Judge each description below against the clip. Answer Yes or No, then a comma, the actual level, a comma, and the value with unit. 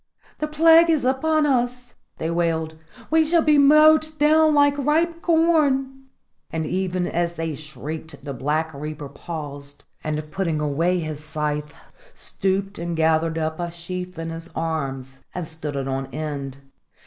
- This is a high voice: No, medium, 170 Hz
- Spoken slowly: No, average, 150 wpm